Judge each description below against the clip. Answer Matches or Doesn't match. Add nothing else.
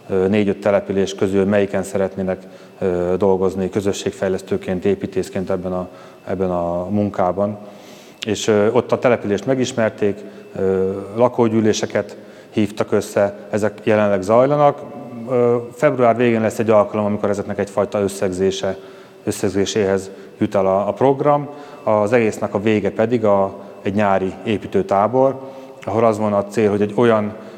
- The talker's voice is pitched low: Matches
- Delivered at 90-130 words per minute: Matches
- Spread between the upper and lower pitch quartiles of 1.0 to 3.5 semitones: Matches